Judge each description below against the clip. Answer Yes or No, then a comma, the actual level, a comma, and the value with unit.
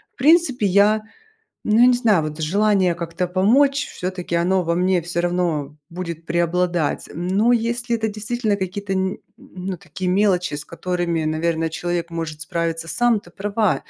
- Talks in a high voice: No, medium, 180 Hz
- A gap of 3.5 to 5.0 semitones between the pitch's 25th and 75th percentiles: Yes, average, 3.9 semitones